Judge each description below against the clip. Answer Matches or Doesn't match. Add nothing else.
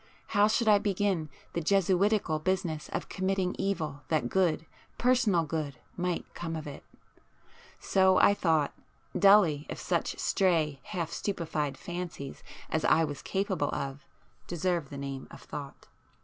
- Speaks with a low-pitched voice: Doesn't match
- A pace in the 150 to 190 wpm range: Doesn't match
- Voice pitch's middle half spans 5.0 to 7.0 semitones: Doesn't match